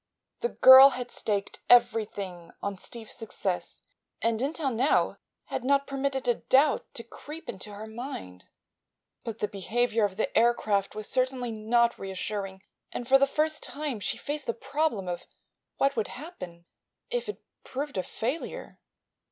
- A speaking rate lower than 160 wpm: Yes, average, 150 wpm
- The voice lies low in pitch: No, high, 235 Hz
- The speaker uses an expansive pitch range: No, average, 4.9 semitones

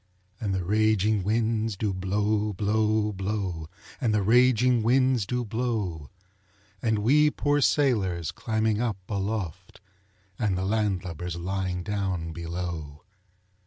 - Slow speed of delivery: Yes, slow, 125 wpm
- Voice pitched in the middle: No, low, 105 Hz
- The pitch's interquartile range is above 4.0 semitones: No, average, 3.2 semitones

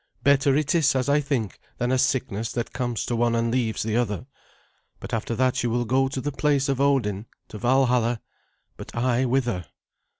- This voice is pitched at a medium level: No, low, 125 Hz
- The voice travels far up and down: No, narrow, 2.6 semitones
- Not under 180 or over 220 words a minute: Yes, average, 195 wpm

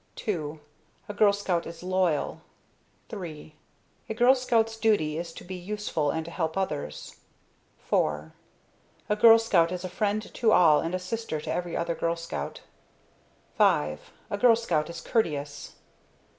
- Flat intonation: No, average, 4.8 semitones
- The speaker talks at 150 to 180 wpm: Yes, average, 155 wpm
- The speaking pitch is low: No, medium, 180 Hz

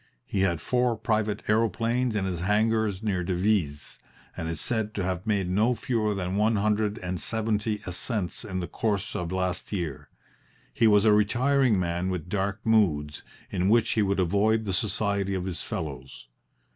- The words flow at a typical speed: Yes, average, 170 wpm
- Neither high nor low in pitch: No, low, 100 Hz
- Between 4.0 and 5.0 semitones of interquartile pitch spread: No, average, 3.1 semitones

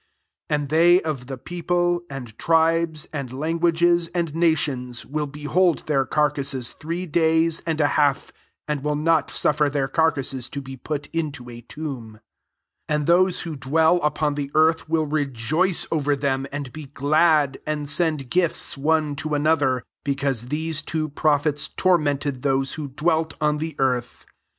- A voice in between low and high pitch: Yes, medium, 150 Hz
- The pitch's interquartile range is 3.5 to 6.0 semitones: No, average, 2.8 semitones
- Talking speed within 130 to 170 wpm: Yes, average, 155 wpm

